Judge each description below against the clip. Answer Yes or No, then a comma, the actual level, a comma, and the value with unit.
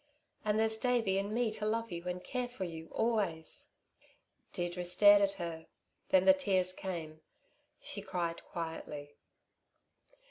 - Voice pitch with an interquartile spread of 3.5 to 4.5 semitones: Yes, average, 4.2 semitones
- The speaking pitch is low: No, high, 190 Hz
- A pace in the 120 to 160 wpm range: Yes, average, 140 wpm